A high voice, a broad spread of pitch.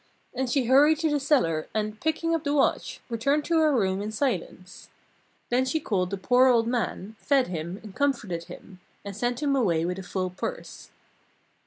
Yes: high, 240 Hz; wide, 6.9 semitones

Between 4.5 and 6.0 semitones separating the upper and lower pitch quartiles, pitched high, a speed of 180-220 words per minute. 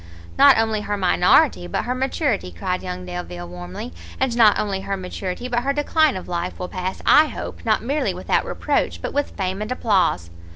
Yes: wide, 5.4 semitones; high, 195 Hz; average, 195 wpm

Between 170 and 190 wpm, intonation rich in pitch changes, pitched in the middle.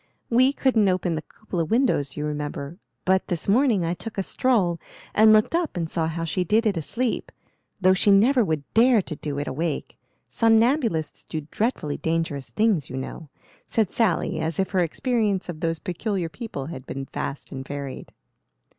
Yes: average, 180 wpm; wide, 6.0 semitones; medium, 180 Hz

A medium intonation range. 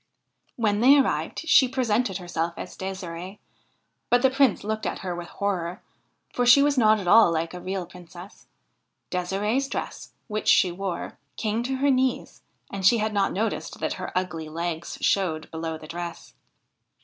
Yes: average, 5.0 semitones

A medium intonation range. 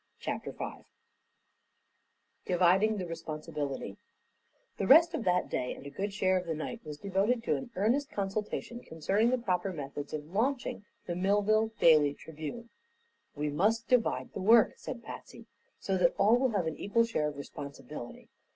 No: wide, 6.4 semitones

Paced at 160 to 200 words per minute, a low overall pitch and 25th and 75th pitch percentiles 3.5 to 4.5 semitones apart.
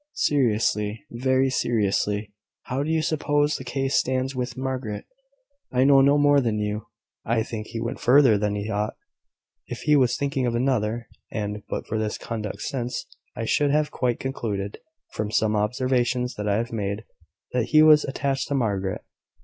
Yes: average, 170 wpm; low, 120 Hz; average, 4.0 semitones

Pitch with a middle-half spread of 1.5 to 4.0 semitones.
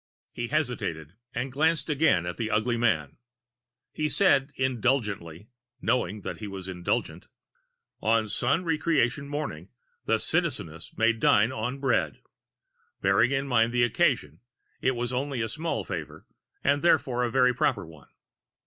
No: average, 5.0 semitones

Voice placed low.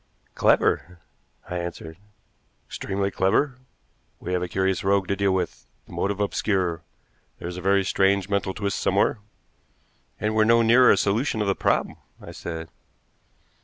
Yes: very low, 95 Hz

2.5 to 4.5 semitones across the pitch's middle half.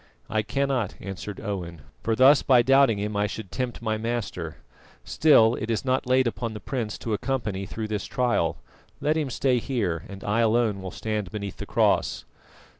Yes: average, 3.7 semitones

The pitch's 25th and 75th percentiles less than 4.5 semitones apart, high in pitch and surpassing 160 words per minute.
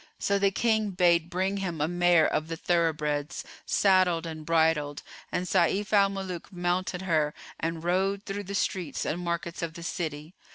No: average, 2.8 semitones; medium, 175 Hz; average, 170 wpm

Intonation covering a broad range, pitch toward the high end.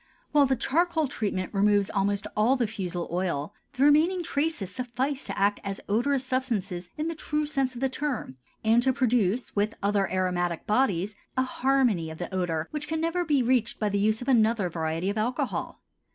Yes: wide, 5.7 semitones; high, 225 Hz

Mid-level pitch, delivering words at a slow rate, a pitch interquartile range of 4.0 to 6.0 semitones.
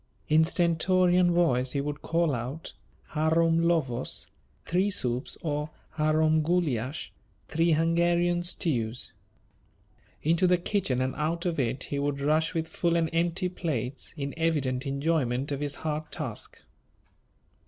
No: medium, 155 Hz; slow, 130 wpm; average, 3.5 semitones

